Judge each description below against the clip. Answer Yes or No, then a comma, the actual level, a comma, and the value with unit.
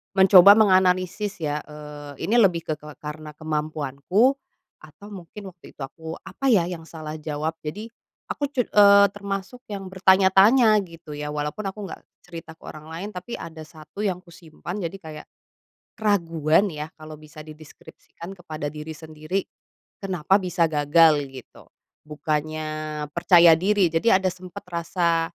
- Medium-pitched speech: Yes, medium, 170 Hz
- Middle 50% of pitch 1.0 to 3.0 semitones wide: No, average, 3.9 semitones